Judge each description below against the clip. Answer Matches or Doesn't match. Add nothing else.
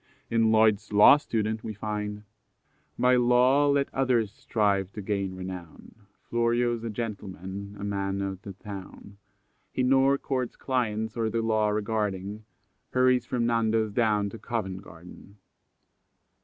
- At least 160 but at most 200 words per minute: Doesn't match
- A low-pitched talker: Matches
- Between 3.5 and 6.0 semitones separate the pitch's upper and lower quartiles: Doesn't match